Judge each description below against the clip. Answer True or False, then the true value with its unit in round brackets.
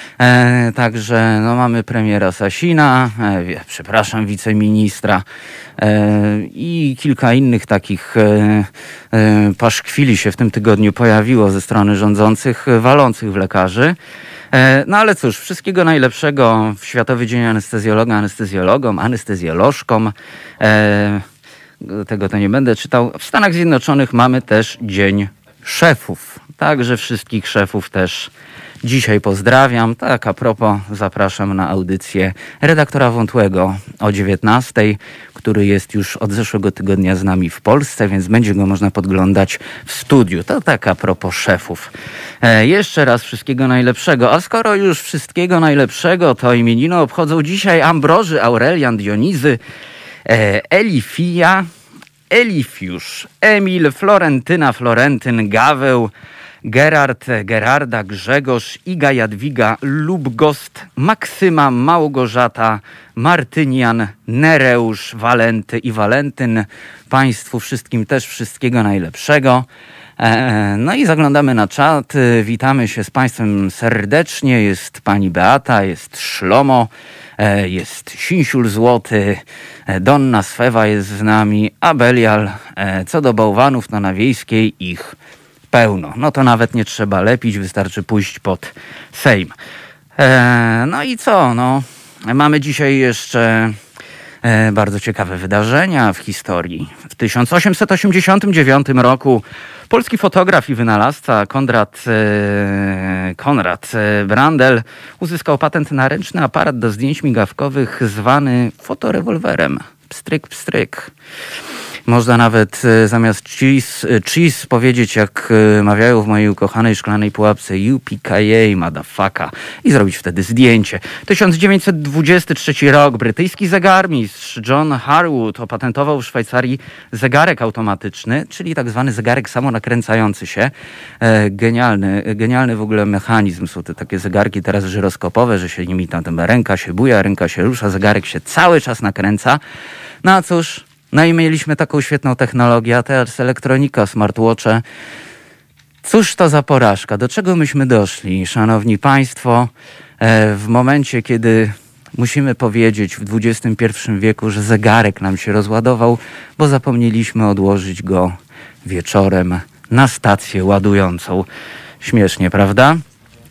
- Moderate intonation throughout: True (4.6 semitones)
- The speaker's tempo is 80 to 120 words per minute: True (115 wpm)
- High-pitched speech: False (115 Hz)